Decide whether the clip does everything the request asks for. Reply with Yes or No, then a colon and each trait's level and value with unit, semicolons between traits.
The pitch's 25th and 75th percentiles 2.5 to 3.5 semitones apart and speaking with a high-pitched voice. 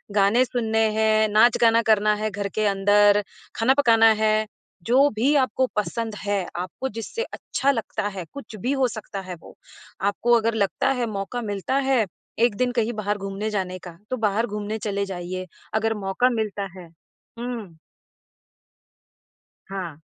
Yes: average, 2.9 semitones; high, 215 Hz